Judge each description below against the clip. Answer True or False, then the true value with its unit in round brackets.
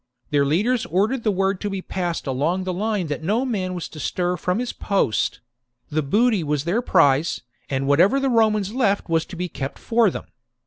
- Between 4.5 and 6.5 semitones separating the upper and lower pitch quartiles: True (5.1 semitones)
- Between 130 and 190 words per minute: False (200 wpm)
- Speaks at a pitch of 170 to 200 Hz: True (185 Hz)